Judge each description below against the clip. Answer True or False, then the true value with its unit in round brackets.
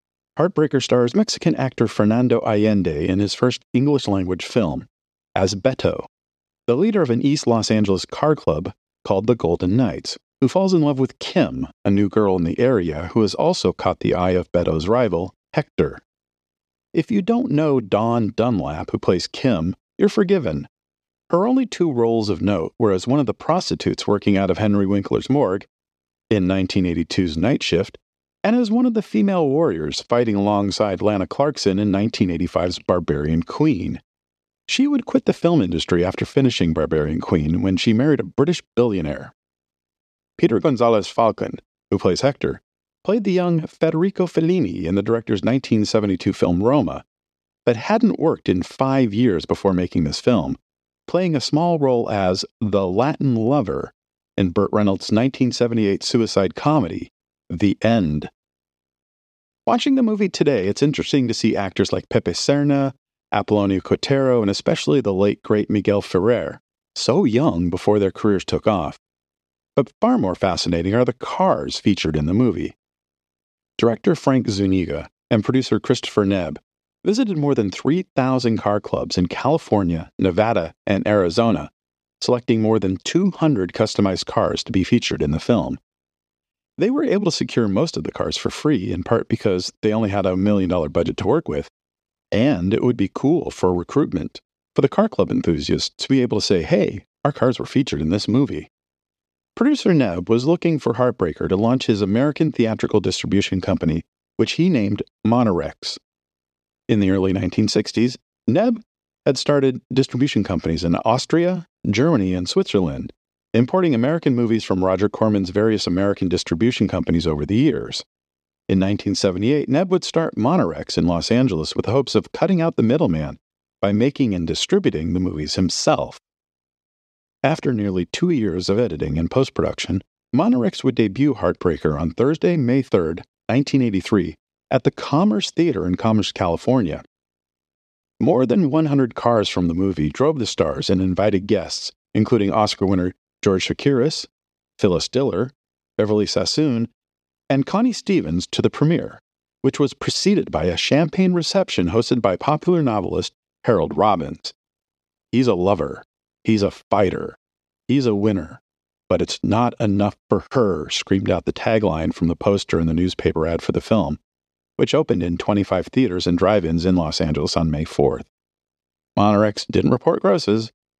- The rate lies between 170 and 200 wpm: False (160 wpm)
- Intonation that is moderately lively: False (6.7 semitones)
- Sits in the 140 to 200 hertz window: False (105 Hz)